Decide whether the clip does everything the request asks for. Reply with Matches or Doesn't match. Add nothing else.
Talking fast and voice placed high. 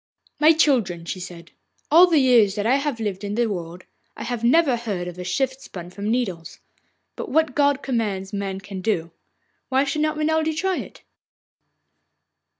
Doesn't match